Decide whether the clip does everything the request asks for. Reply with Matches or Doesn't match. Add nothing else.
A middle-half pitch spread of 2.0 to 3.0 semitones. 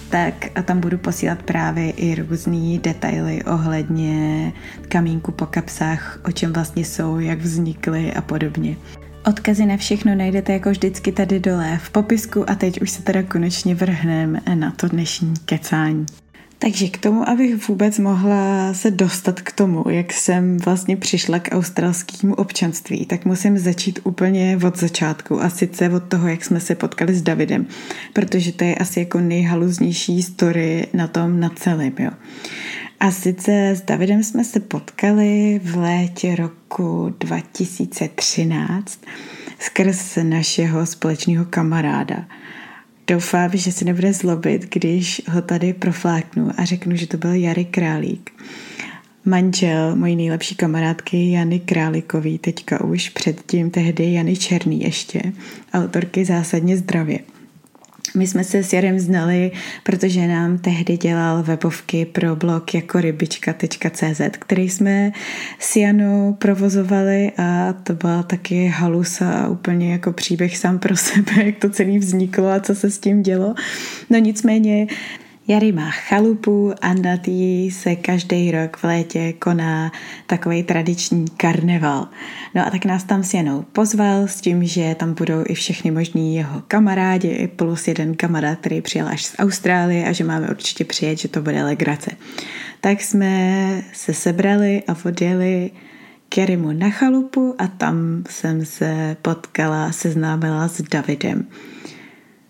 Matches